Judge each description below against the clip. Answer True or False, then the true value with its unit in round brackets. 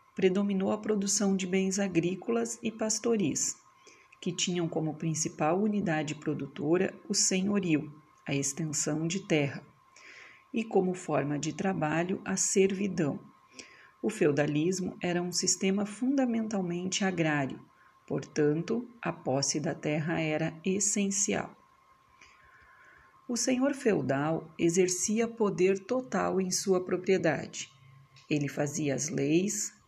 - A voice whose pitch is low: False (185 Hz)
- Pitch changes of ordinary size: True (4.6 semitones)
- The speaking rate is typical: False (110 wpm)